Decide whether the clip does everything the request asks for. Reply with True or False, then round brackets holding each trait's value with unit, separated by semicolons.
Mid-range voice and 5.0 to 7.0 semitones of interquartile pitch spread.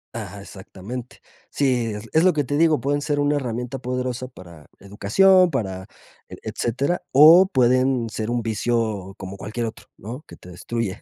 False (120 Hz; 5.3 semitones)